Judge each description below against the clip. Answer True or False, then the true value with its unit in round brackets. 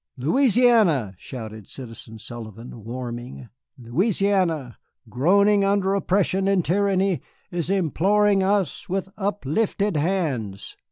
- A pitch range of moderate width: False (8.2 semitones)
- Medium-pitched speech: True (180 Hz)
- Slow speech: True (95 wpm)